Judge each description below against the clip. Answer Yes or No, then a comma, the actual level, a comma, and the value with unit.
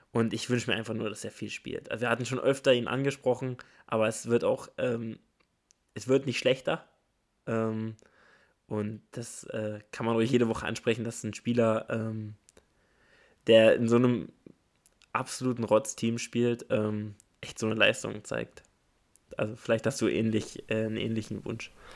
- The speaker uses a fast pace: No, average, 170 wpm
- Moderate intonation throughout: No, narrow, 1.5 semitones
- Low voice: Yes, low, 115 Hz